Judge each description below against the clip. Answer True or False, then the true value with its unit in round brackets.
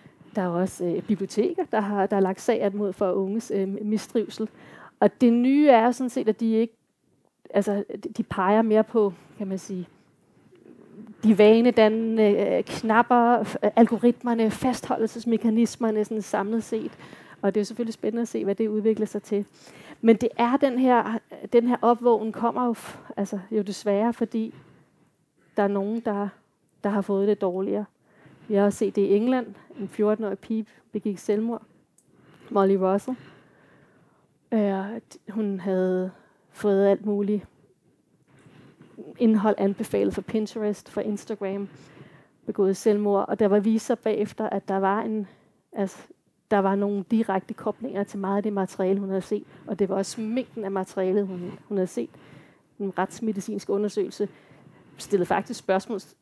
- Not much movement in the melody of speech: True (2.2 semitones)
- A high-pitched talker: True (210 Hz)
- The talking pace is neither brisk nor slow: True (155 wpm)